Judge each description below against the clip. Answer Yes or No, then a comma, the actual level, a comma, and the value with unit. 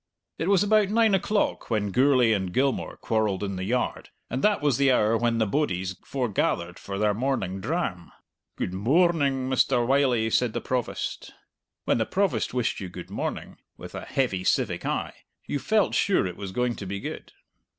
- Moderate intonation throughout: No, wide, 6.0 semitones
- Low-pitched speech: Yes, low, 120 Hz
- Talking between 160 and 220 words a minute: Yes, average, 180 wpm